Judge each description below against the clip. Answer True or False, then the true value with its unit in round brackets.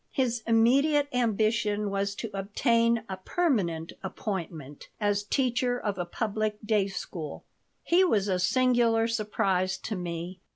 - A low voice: False (210 Hz)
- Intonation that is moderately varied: True (3.6 semitones)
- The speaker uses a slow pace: True (130 wpm)